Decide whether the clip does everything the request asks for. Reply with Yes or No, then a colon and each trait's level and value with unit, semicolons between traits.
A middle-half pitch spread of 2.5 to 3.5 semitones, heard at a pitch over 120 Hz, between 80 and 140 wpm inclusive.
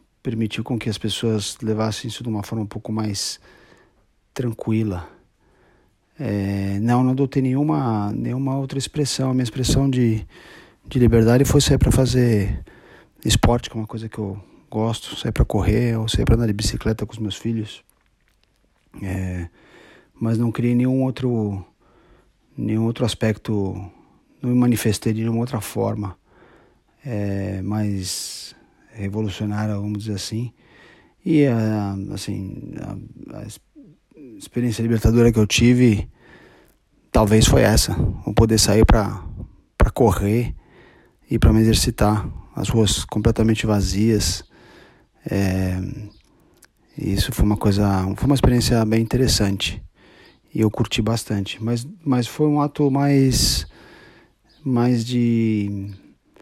No: average, 2.8 semitones; low, 110 Hz; average, 130 wpm